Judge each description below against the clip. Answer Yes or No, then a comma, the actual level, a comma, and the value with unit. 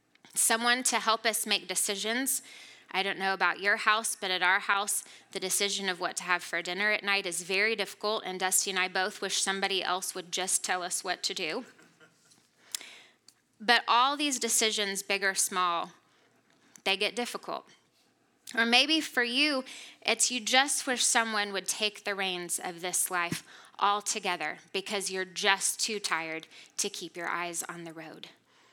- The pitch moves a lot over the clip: No, average, 3.6 semitones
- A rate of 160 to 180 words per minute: Yes, average, 175 wpm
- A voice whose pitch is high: Yes, high, 200 Hz